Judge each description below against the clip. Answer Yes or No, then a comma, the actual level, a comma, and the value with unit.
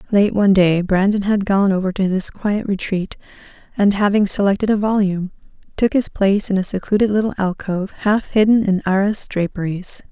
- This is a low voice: No, high, 200 Hz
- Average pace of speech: Yes, average, 170 wpm